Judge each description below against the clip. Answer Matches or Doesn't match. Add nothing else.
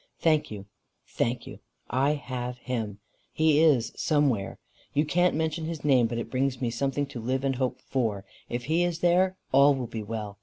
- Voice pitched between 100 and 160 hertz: Matches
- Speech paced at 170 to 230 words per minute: Matches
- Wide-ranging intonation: Doesn't match